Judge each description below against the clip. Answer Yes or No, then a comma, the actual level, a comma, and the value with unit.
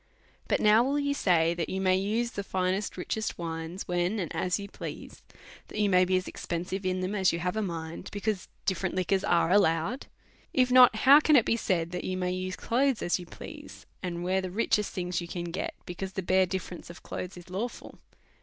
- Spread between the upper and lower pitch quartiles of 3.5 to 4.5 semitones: No, average, 2.9 semitones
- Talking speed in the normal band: No, fast, 220 wpm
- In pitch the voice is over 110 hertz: Yes, medium, 185 Hz